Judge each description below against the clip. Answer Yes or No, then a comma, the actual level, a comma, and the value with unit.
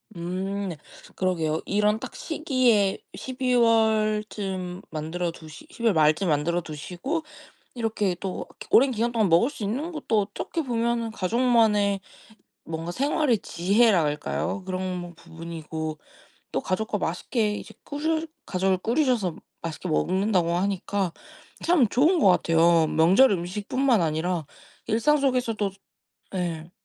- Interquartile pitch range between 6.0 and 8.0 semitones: No, average, 5.3 semitones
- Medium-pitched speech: No, high, 200 Hz